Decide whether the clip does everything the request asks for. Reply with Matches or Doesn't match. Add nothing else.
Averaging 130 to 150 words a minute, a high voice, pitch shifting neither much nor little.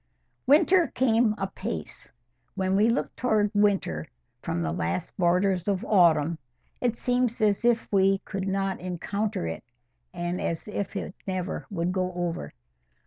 Matches